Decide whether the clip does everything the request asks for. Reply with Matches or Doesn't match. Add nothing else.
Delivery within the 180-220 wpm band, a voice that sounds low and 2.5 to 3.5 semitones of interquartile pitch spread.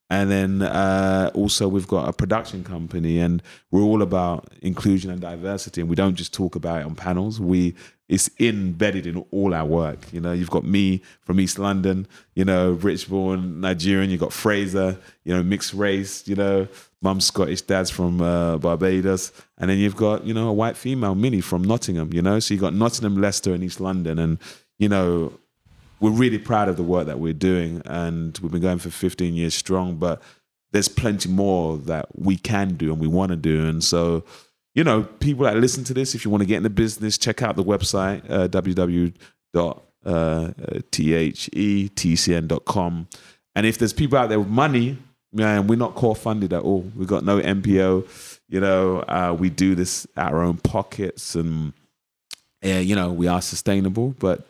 Matches